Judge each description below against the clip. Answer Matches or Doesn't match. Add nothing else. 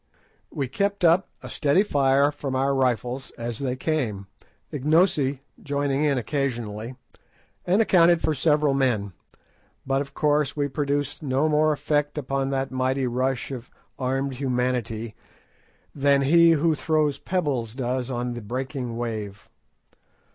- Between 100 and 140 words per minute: Matches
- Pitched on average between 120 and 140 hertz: Matches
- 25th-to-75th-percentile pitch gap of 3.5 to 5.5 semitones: Doesn't match